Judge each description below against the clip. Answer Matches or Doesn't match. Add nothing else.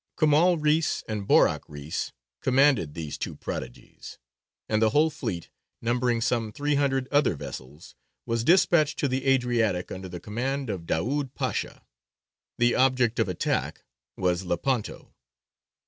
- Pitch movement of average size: Doesn't match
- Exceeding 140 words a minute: Doesn't match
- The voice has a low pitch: Matches